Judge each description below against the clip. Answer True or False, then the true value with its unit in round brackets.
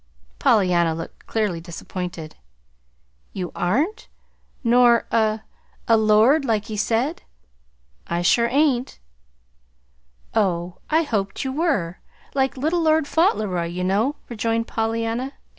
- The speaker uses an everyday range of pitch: False (6.3 semitones)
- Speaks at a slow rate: True (115 wpm)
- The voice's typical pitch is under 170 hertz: False (225 Hz)